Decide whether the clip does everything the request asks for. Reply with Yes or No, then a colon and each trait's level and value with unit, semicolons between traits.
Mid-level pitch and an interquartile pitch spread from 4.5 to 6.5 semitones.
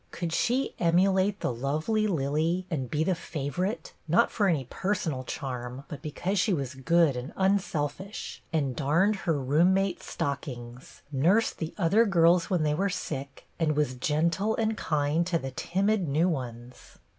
Yes: medium, 165 Hz; average, 5.3 semitones